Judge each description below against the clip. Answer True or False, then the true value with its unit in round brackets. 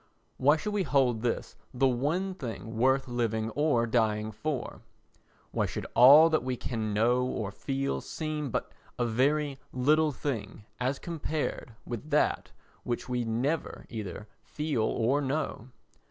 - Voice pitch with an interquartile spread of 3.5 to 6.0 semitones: True (4.5 semitones)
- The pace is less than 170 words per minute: True (145 wpm)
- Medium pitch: False (125 Hz)